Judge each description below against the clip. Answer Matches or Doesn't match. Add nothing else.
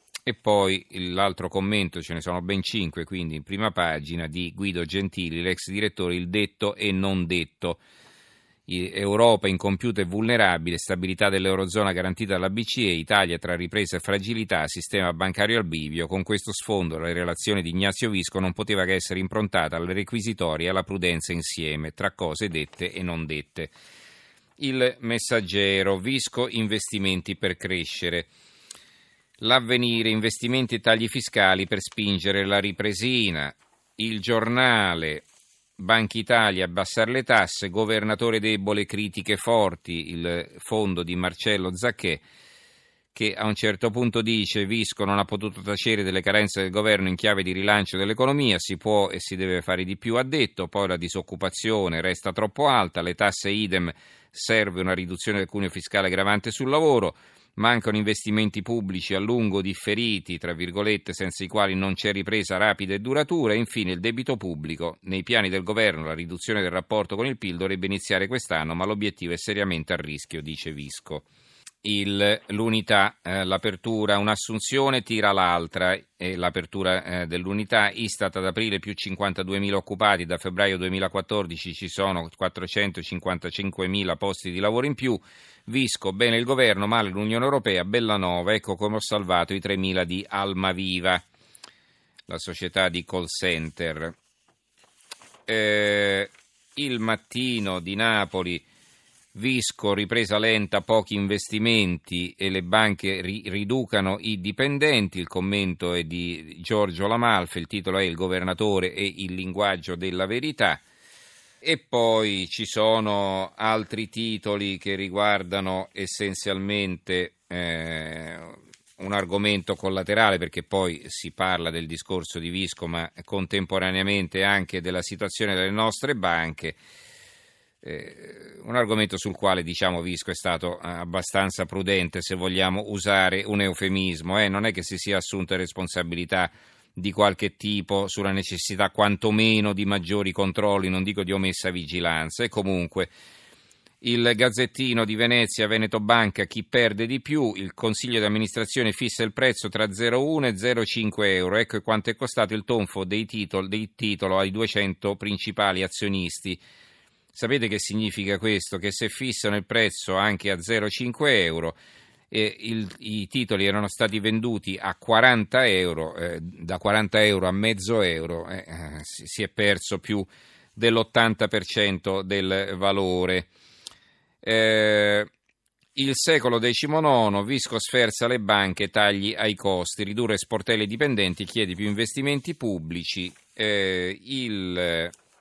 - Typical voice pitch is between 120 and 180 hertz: Doesn't match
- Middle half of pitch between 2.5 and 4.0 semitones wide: Matches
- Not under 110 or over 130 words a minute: Doesn't match